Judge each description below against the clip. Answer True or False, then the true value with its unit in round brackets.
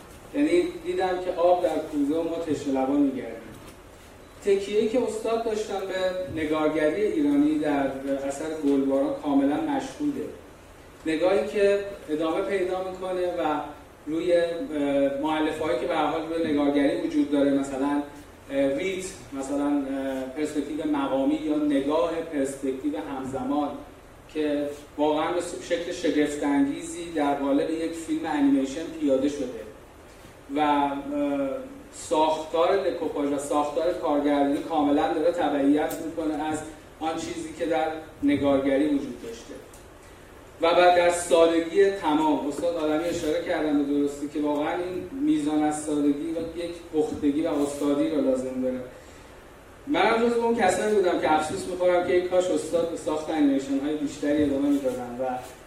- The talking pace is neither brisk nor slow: True (130 wpm)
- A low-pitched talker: False (160 Hz)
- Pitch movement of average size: True (4.3 semitones)